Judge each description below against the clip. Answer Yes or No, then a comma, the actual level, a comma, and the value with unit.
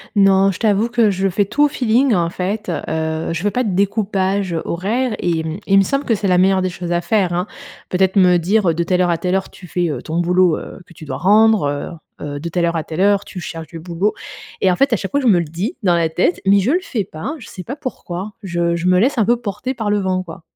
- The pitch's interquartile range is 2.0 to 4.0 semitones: Yes, average, 3.5 semitones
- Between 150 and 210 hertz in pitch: Yes, medium, 185 Hz